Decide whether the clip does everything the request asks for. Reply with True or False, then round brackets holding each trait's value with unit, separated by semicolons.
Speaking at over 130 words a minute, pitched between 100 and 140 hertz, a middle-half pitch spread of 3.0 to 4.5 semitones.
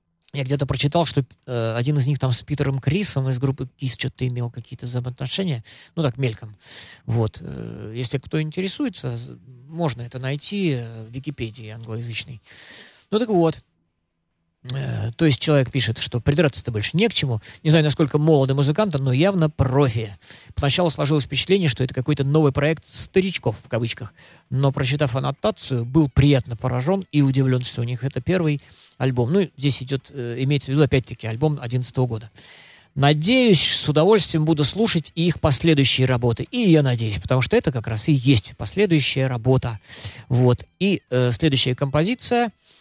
True (155 wpm; 135 Hz; 4.1 semitones)